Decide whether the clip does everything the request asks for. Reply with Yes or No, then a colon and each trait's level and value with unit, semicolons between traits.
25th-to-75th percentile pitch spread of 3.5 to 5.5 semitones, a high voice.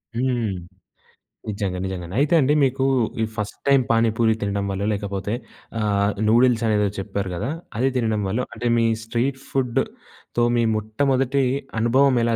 No: average, 3.8 semitones; low, 115 Hz